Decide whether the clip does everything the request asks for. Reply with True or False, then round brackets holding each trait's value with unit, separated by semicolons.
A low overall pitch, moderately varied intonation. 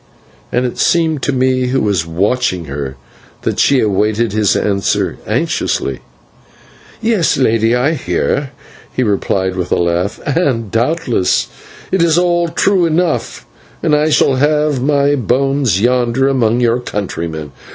False (125 Hz; 6.1 semitones)